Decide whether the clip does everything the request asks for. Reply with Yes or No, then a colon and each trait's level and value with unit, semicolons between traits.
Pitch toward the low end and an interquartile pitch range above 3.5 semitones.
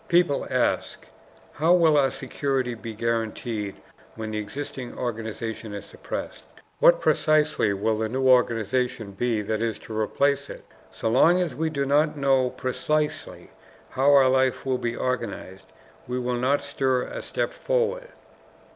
Yes: low, 130 Hz; average, 4.2 semitones